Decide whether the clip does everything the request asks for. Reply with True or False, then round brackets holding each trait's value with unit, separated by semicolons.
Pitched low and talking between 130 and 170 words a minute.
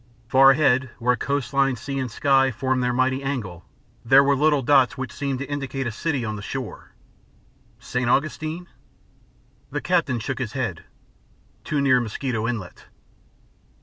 True (130 Hz; 155 wpm)